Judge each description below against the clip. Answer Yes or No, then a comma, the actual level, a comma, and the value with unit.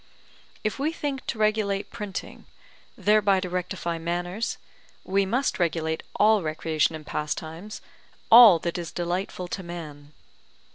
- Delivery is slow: Yes, slow, 130 wpm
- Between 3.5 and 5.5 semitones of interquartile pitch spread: Yes, average, 4.3 semitones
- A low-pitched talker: No, medium, 180 Hz